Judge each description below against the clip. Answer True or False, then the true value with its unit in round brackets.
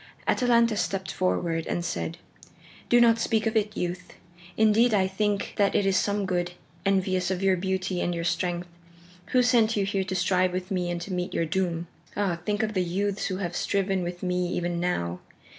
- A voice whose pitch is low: False (185 Hz)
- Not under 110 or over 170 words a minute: False (195 wpm)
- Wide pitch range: False (2.5 semitones)